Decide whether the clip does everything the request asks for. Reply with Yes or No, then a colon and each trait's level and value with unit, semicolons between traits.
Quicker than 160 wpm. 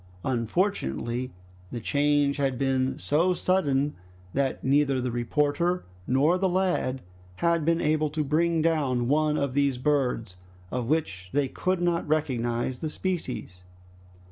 No: slow, 135 wpm